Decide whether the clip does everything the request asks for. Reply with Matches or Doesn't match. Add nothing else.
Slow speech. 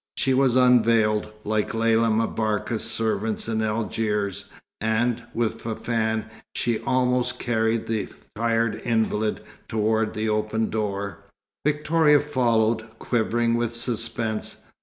Matches